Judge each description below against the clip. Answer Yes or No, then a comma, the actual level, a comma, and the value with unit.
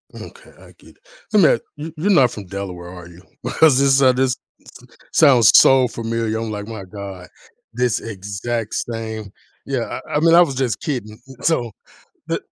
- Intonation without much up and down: No, average, 4.6 semitones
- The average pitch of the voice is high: No, low, 115 Hz